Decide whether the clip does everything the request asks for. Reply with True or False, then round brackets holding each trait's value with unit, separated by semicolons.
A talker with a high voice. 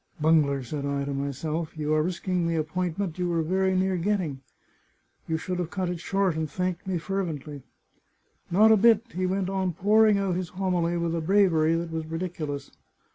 False (175 Hz)